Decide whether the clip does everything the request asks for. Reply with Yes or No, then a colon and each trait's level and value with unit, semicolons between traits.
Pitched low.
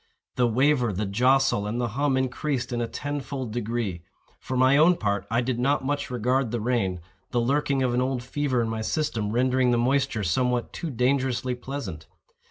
Yes: low, 125 Hz